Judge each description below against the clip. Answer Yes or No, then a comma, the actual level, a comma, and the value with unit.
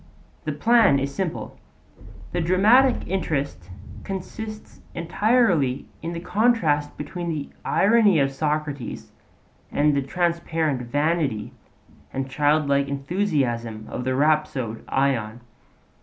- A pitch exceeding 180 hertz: No, medium, 150 Hz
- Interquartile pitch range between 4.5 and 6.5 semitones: Yes, average, 4.8 semitones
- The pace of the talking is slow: Yes, slow, 105 wpm